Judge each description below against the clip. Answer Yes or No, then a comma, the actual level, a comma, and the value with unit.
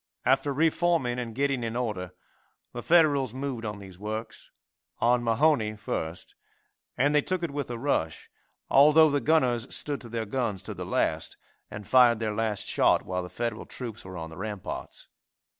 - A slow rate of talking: No, average, 175 wpm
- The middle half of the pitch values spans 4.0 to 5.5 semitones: Yes, average, 4.8 semitones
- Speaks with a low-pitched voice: Yes, low, 120 Hz